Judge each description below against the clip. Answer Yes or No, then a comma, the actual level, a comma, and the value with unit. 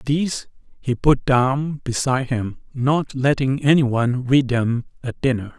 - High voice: No, low, 130 Hz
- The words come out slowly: Yes, slow, 130 wpm